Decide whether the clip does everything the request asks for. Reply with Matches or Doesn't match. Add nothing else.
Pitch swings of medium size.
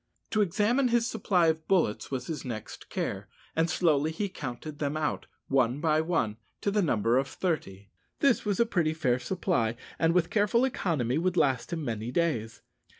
Doesn't match